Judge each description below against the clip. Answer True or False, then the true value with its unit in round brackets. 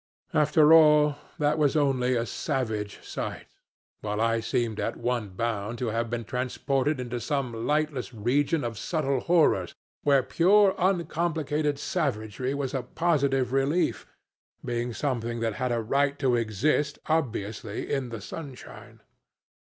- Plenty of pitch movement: False (4.2 semitones)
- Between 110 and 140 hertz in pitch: True (135 Hz)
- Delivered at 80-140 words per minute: True (135 wpm)